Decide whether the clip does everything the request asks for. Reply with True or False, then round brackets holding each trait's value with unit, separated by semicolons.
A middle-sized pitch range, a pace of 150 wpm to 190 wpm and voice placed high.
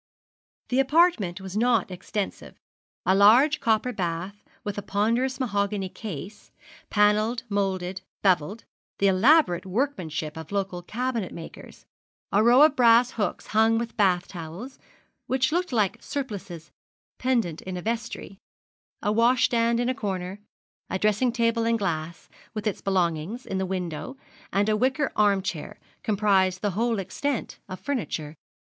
False (4.1 semitones; 140 wpm; 210 Hz)